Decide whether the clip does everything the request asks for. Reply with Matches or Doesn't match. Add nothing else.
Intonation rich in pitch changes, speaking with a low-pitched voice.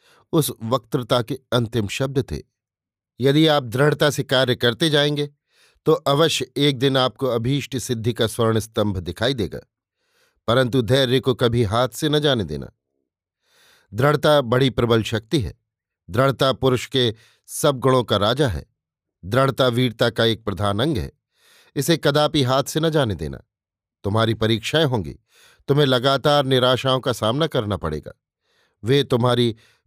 Doesn't match